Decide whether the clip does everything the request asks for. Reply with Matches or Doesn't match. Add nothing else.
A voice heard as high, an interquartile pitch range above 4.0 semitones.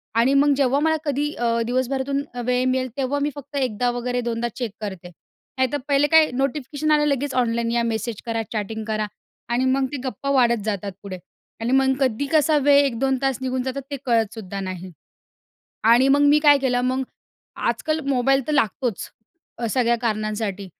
Doesn't match